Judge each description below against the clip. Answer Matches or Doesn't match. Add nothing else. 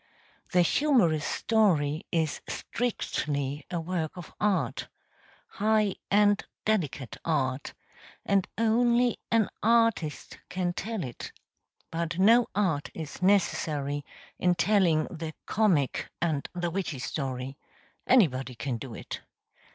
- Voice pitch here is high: Doesn't match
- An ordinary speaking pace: Doesn't match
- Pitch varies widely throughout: Matches